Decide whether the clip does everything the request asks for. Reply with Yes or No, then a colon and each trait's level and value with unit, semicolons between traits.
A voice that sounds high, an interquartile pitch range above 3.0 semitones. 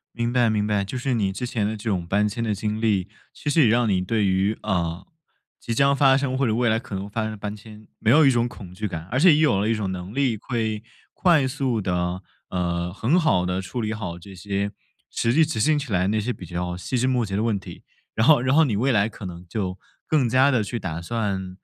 No: low, 110 Hz; average, 4.4 semitones